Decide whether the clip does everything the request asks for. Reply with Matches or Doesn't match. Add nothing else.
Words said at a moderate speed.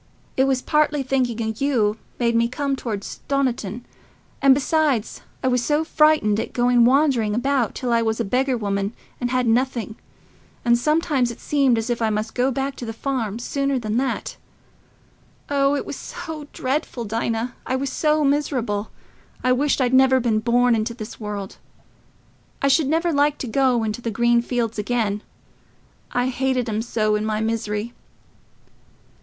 Matches